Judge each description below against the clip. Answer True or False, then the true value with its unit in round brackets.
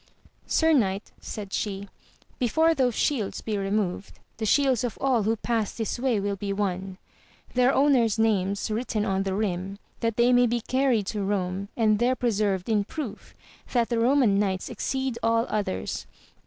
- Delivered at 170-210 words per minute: True (175 wpm)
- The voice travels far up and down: False (3.7 semitones)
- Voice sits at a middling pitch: False (220 Hz)